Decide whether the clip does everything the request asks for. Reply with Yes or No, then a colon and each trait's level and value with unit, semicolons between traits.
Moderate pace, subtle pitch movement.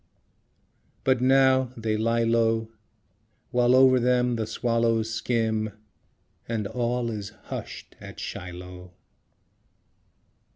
No: slow, 95 wpm; narrow, 2.0 semitones